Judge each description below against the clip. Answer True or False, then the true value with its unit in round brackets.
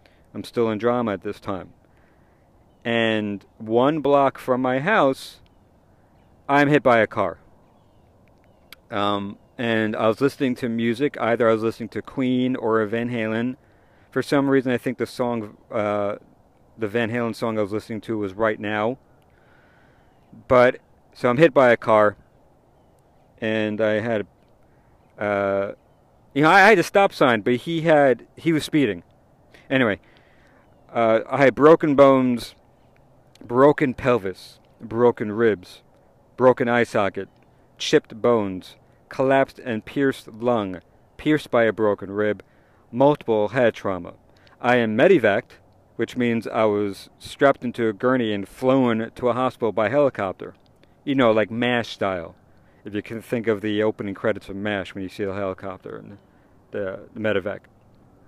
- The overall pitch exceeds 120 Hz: False (115 Hz)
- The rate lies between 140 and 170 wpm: True (150 wpm)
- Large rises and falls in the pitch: False (3.6 semitones)